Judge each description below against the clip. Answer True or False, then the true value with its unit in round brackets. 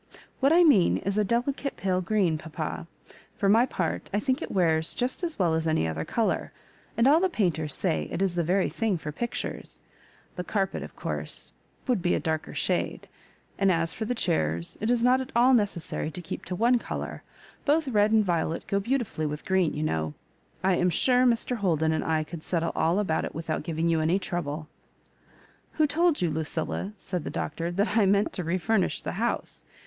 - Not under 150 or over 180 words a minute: False (205 wpm)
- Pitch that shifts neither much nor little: False (6.2 semitones)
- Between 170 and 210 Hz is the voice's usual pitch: True (185 Hz)